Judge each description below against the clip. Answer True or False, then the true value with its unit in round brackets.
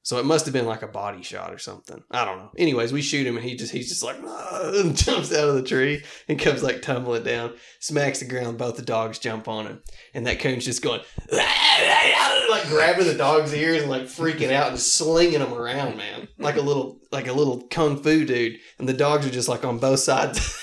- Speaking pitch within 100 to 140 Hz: True (135 Hz)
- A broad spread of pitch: False (4.0 semitones)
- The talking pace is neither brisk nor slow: False (235 wpm)